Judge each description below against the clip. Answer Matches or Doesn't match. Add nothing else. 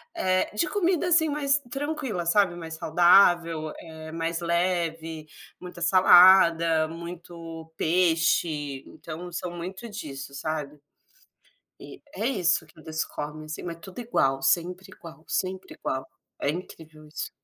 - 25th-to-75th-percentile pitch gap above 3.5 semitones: Doesn't match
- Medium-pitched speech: Matches